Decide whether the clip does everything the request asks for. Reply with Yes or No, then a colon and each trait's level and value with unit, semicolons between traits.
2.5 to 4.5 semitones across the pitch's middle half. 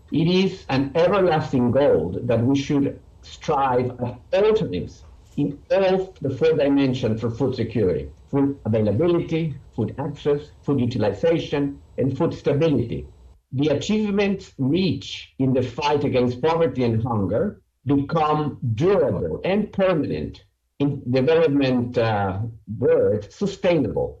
No: average, 4.9 semitones